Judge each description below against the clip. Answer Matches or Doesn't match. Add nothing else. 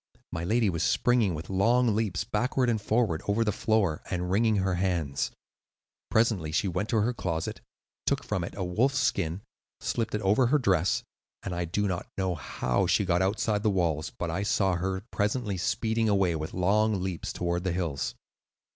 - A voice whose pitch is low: Matches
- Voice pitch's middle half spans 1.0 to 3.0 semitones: Doesn't match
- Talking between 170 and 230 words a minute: Matches